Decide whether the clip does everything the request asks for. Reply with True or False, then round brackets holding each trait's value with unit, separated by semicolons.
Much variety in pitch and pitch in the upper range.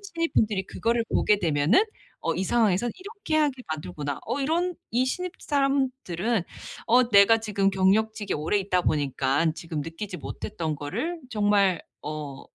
True (7.5 semitones; 205 Hz)